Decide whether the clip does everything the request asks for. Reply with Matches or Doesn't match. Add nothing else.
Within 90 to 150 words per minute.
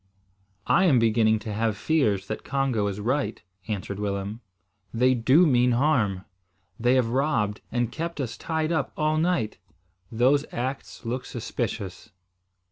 Matches